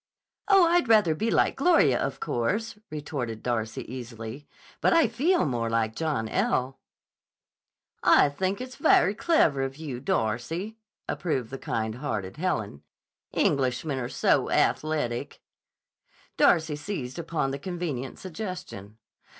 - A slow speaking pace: Yes, slow, 125 wpm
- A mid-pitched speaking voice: Yes, medium, 145 Hz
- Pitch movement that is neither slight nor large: No, wide, 7.6 semitones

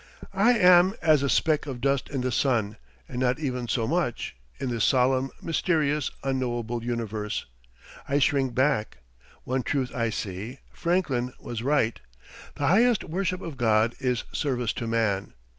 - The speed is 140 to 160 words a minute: Yes, average, 155 wpm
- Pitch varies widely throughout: No, average, 4.0 semitones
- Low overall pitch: Yes, low, 130 Hz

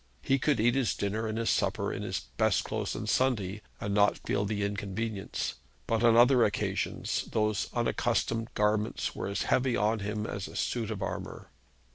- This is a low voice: Yes, low, 110 Hz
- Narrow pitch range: Yes, narrow, 2.1 semitones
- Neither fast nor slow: Yes, average, 180 wpm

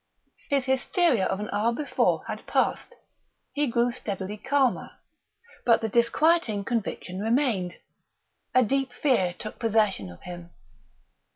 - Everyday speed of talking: No, slow, 125 wpm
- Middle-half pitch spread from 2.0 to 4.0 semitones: No, average, 4.9 semitones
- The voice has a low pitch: No, high, 230 Hz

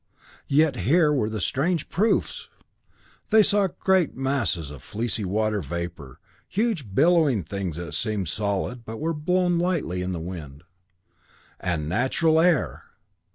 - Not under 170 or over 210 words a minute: No, slow, 135 wpm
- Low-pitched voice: Yes, low, 115 Hz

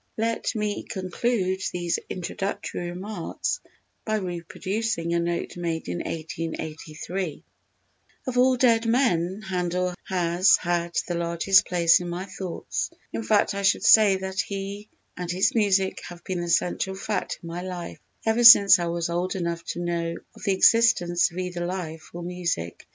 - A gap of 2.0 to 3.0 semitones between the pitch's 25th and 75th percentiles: Yes, narrow, 2.6 semitones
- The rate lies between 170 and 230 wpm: No, average, 155 wpm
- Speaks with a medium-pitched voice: Yes, medium, 180 Hz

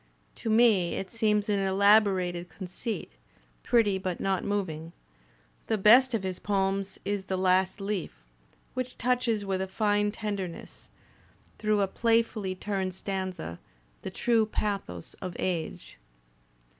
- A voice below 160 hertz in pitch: No, high, 195 Hz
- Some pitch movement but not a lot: No, narrow, 2.3 semitones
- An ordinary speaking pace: No, slow, 130 wpm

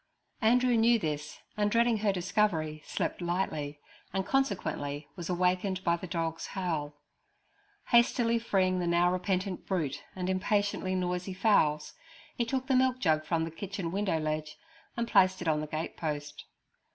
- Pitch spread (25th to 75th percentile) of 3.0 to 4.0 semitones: No, average, 4.5 semitones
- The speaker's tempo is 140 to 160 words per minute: Yes, average, 155 wpm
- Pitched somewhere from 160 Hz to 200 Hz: Yes, medium, 185 Hz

